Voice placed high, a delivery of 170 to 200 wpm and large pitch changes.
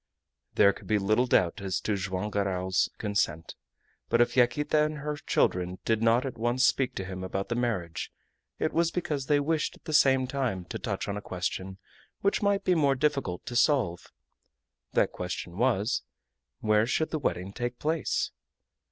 No: low, 120 Hz; average, 180 wpm; wide, 6.7 semitones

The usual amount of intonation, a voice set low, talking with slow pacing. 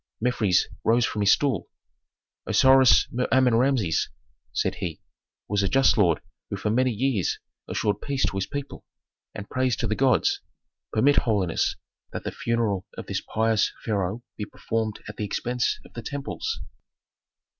No: average, 4.0 semitones; low, 115 Hz; average, 155 wpm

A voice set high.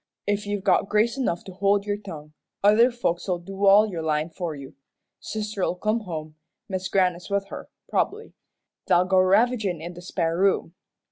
Yes: high, 195 Hz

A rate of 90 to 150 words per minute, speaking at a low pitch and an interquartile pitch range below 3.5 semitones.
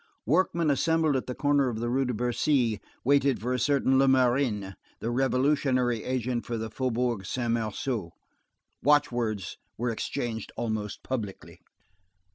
Yes: average, 140 wpm; low, 125 Hz; average, 3.0 semitones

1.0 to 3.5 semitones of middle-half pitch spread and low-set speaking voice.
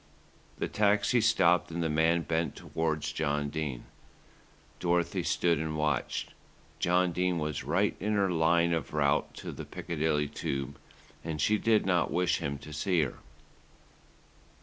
Yes: narrow, 2.6 semitones; very low, 80 Hz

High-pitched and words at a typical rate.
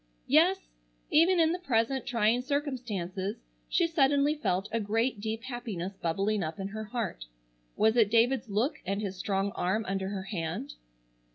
Yes: high, 220 Hz; average, 160 wpm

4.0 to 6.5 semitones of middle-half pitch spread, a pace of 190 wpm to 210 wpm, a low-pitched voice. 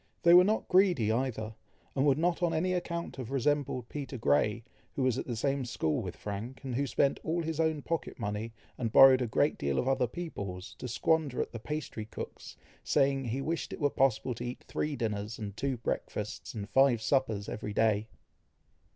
Yes: average, 5.1 semitones; average, 200 wpm; low, 130 Hz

